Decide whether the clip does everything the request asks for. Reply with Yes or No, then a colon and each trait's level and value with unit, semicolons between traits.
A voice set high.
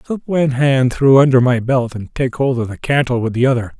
No: low, 130 Hz